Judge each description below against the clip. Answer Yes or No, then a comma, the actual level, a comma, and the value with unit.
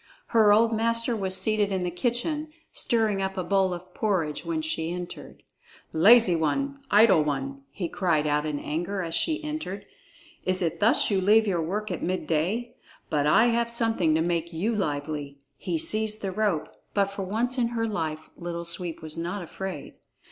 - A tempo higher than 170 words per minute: Yes, average, 180 wpm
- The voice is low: No, high, 190 Hz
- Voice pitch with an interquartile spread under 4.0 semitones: No, average, 5.2 semitones